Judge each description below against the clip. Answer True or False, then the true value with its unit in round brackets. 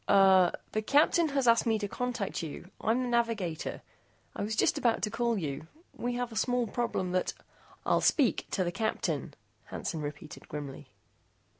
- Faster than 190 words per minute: False (175 wpm)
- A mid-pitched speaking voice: False (220 Hz)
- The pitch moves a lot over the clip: False (4.9 semitones)